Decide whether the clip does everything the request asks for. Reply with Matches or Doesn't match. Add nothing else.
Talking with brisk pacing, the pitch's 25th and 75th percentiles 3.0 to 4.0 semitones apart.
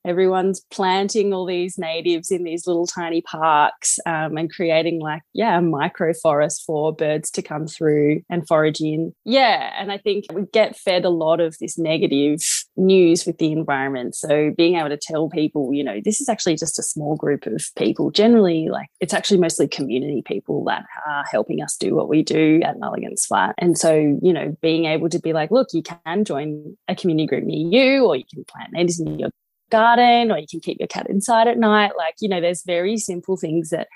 Matches